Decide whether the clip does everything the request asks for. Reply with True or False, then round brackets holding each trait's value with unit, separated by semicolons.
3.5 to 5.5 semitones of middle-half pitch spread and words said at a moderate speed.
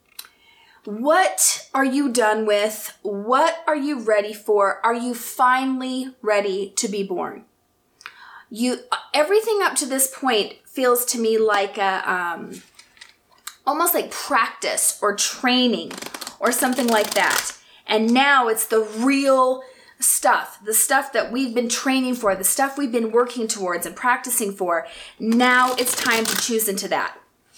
True (3.8 semitones; 145 wpm)